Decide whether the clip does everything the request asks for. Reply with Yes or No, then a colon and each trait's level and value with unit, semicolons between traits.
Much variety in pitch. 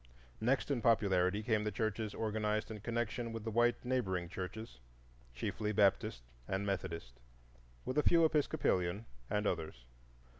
No: average, 3.4 semitones